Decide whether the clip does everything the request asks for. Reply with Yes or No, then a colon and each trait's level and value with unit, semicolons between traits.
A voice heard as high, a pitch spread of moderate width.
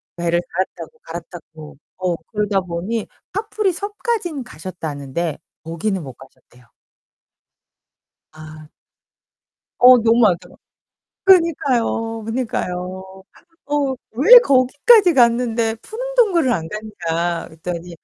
No: high, 210 Hz; wide, 7.6 semitones